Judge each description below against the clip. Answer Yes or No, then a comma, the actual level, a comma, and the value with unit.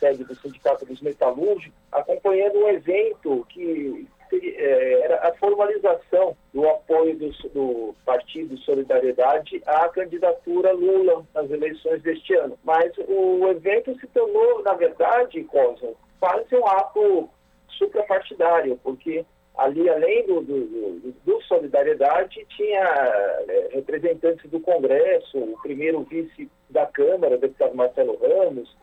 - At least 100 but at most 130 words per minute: Yes, slow, 120 wpm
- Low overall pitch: No, very high, 270 Hz